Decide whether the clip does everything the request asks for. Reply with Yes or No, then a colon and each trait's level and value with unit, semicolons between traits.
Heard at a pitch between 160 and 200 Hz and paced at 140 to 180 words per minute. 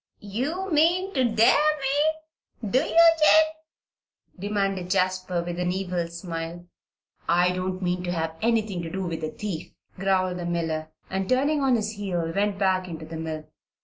Yes: high, 190 Hz; average, 165 wpm